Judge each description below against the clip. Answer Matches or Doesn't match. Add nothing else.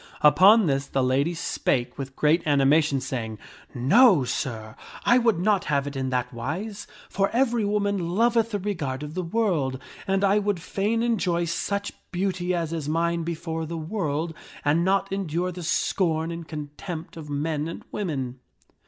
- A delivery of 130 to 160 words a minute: Doesn't match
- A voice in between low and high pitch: Matches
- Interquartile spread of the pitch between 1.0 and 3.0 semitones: Doesn't match